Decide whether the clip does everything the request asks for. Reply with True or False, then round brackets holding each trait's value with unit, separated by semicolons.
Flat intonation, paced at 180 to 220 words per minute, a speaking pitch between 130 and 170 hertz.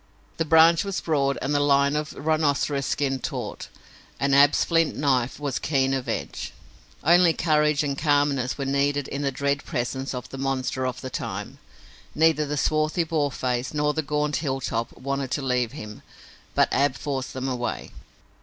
False (2.1 semitones; 170 wpm; 140 Hz)